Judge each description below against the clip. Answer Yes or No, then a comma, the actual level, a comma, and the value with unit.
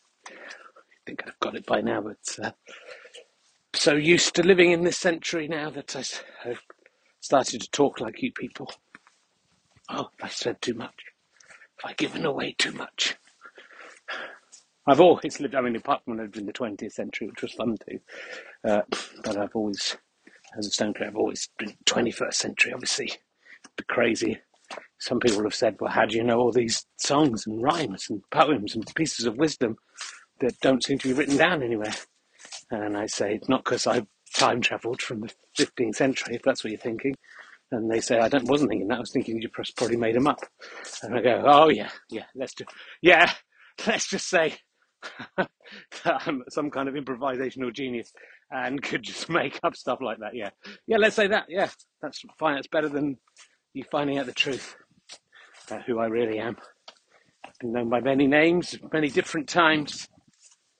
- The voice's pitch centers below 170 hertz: Yes, low, 135 Hz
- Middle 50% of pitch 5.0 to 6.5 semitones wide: Yes, wide, 5.4 semitones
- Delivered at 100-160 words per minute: No, average, 190 wpm